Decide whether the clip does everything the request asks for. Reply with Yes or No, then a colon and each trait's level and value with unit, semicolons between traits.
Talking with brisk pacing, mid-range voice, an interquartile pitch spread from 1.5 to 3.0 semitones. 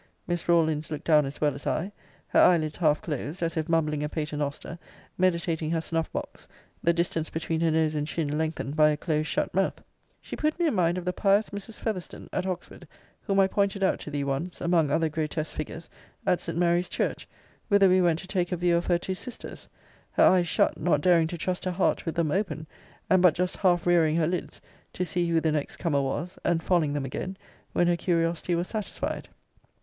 Yes: fast, 215 wpm; medium, 170 Hz; narrow, 2.6 semitones